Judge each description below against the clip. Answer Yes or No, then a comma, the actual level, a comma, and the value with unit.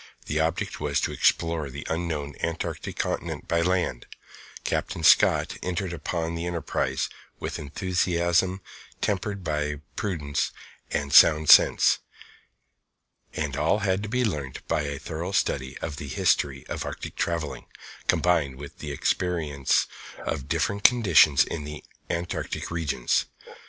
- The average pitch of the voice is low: Yes, very low, 80 Hz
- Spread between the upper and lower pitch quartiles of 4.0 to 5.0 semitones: No, average, 3.5 semitones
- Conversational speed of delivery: No, slow, 125 wpm